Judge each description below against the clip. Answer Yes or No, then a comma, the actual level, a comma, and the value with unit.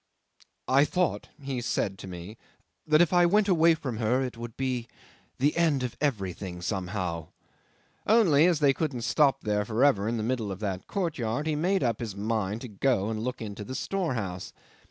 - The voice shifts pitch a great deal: Yes, wide, 6.3 semitones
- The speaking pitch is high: No, low, 125 Hz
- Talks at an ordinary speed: Yes, average, 190 wpm